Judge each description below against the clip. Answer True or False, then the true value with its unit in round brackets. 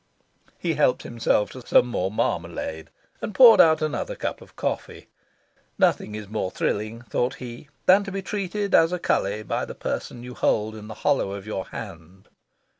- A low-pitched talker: True (120 Hz)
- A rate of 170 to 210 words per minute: True (180 wpm)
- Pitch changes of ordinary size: False (7.6 semitones)